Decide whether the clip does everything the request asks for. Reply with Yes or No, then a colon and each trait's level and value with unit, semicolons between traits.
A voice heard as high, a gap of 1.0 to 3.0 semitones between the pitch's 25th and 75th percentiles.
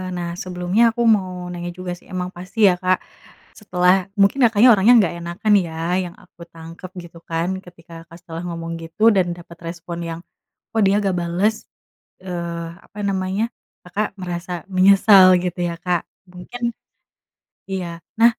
No: medium, 180 Hz; narrow, 2.4 semitones